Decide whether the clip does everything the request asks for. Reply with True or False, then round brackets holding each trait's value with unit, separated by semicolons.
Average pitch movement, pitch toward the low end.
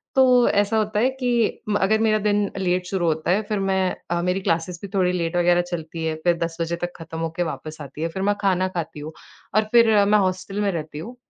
False (3.6 semitones; 180 Hz)